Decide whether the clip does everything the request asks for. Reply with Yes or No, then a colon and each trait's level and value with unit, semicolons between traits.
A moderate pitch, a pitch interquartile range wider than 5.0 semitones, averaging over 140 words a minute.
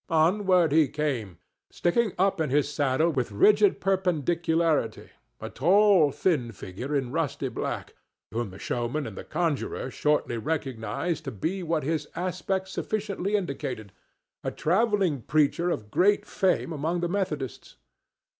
No: medium, 160 Hz; wide, 5.5 semitones; slow, 135 wpm